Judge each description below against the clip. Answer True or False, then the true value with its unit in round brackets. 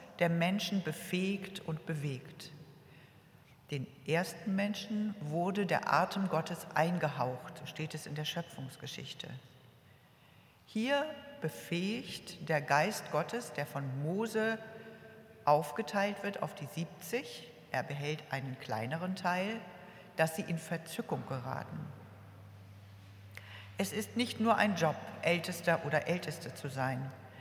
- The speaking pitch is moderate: True (160 Hz)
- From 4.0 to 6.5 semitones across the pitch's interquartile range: True (5.5 semitones)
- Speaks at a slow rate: True (115 wpm)